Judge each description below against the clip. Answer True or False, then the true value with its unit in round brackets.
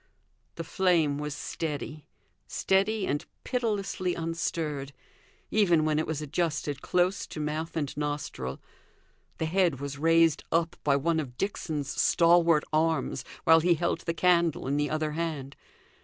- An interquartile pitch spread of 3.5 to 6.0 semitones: False (2.5 semitones)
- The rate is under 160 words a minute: True (140 wpm)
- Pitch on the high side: False (160 Hz)